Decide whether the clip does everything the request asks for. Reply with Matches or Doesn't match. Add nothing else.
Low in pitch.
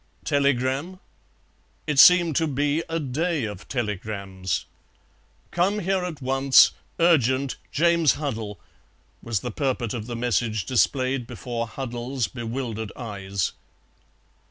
Matches